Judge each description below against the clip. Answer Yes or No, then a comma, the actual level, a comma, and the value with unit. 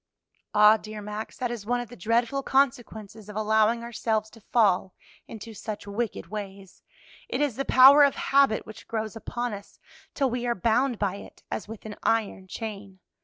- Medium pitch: No, high, 220 Hz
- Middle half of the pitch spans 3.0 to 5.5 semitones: No, narrow, 2.5 semitones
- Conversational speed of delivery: Yes, average, 180 wpm